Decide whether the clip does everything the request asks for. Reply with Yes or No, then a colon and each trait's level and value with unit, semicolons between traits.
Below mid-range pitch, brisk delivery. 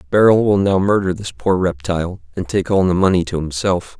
Yes: very low, 90 Hz; fast, 210 wpm